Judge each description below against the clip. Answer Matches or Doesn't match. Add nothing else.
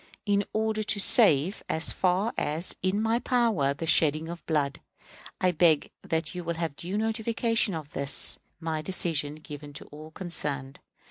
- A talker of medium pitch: Matches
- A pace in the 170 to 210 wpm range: Doesn't match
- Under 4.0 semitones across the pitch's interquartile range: Doesn't match